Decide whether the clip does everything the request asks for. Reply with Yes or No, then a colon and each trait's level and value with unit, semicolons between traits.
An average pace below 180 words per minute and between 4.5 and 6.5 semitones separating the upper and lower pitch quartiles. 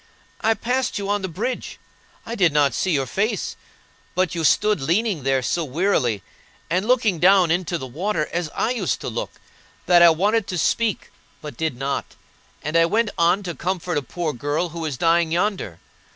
No: average, 190 wpm; average, 4.8 semitones